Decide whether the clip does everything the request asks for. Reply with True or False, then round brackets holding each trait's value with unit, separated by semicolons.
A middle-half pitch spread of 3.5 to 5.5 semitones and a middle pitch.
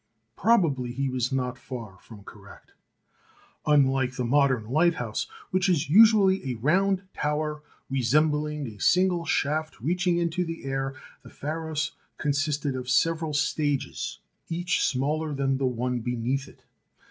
True (4.1 semitones; 145 Hz)